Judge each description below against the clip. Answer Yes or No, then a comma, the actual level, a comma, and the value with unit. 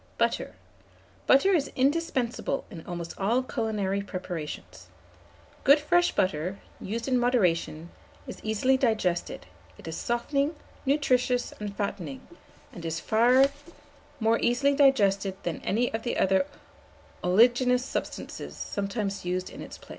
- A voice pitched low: No, high, 220 Hz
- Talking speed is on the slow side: Yes, slow, 125 wpm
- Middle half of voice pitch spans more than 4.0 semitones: Yes, wide, 5.6 semitones